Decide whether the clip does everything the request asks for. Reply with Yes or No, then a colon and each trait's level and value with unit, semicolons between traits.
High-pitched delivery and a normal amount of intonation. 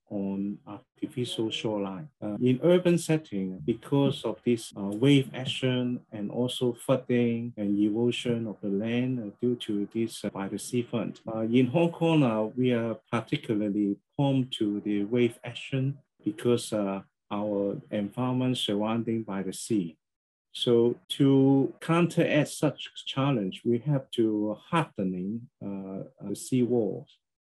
No: low, 120 Hz; average, 3.9 semitones